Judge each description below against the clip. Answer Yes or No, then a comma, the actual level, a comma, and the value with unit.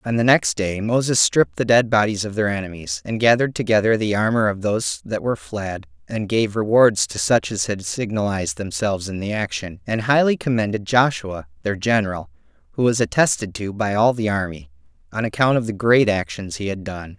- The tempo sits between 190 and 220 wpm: Yes, average, 200 wpm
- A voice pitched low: Yes, low, 105 Hz